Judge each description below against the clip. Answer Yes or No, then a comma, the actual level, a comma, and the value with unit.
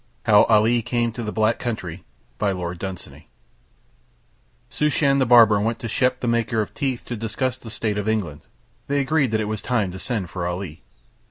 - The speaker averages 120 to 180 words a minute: Yes, average, 175 wpm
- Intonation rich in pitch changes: No, average, 3.1 semitones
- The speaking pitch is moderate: No, low, 110 Hz